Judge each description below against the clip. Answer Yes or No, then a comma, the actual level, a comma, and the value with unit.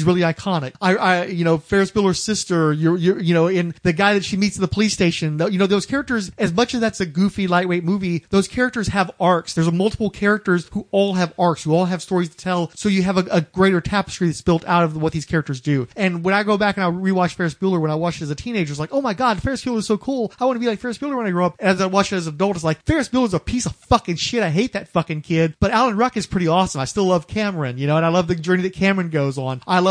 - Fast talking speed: Yes, fast, 305 wpm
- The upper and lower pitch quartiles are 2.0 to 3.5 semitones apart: Yes, average, 3.2 semitones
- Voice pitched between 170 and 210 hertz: Yes, medium, 185 Hz